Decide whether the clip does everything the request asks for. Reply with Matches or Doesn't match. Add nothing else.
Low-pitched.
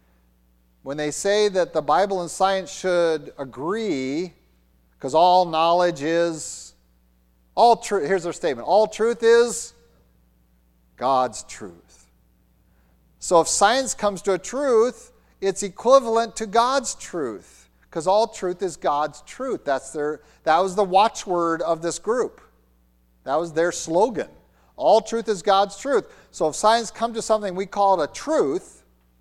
Doesn't match